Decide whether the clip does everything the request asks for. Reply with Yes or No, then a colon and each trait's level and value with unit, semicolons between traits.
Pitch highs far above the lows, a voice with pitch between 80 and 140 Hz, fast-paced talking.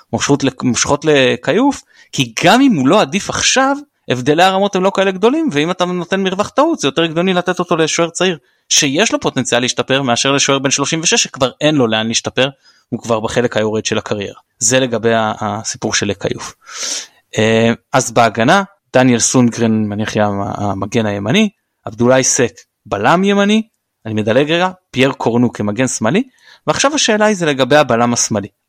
Yes: wide, 8.1 semitones; low, 135 Hz; fast, 160 wpm